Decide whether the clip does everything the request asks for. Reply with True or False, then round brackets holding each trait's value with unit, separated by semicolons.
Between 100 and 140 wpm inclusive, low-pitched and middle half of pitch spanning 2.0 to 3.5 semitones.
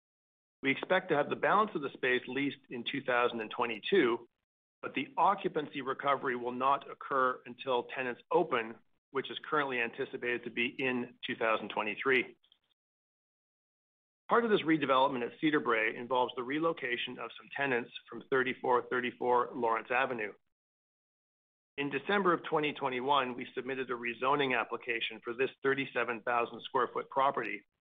True (135 wpm; 125 Hz; 2.7 semitones)